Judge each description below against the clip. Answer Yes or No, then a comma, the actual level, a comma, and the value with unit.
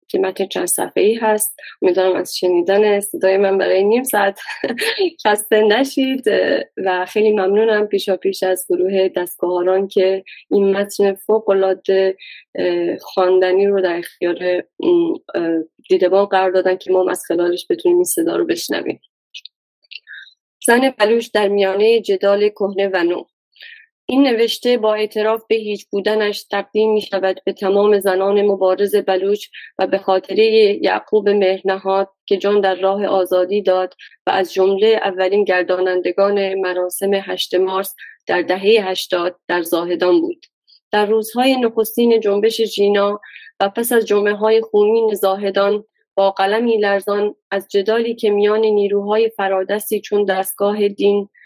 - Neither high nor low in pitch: No, high, 200 Hz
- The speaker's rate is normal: Yes, average, 135 wpm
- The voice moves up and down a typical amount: No, narrow, 2.2 semitones